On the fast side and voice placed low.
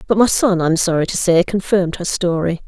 No: fast, 245 wpm; medium, 180 Hz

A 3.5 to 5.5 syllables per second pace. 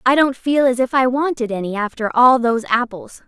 Yes: 5.4 syllables/s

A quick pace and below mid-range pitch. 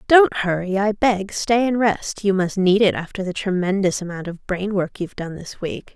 No: fast, 220 wpm; high, 195 Hz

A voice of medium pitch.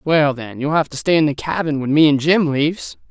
Yes: medium, 150 Hz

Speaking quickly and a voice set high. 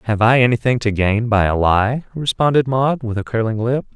No: fast, 210 wpm; low, 115 Hz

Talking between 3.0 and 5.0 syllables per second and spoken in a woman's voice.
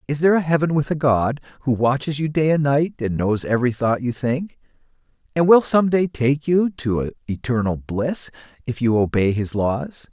No: 4.8 syllables/s; male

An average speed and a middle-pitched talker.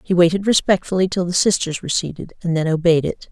No: fast, 220 wpm; medium, 175 Hz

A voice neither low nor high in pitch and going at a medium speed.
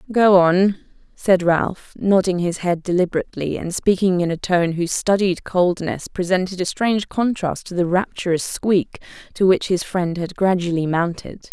Yes: medium, 180 Hz; average, 160 wpm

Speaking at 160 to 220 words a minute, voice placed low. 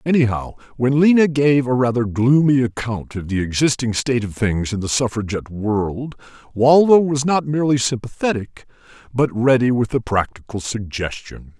No: average, 150 wpm; low, 120 Hz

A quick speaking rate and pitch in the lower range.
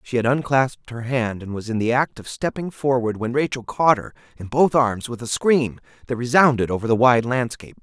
Yes: fast, 220 wpm; low, 125 Hz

